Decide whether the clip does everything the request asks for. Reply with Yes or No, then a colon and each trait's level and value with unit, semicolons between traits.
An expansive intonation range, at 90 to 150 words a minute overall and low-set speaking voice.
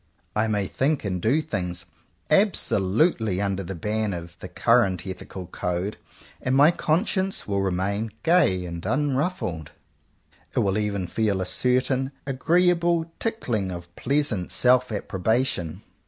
Yes: wide, 7.0 semitones; average, 140 wpm; low, 105 Hz